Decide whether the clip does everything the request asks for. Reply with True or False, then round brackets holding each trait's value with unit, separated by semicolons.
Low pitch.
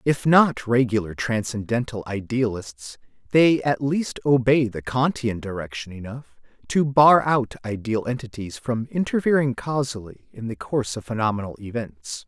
True (120 Hz)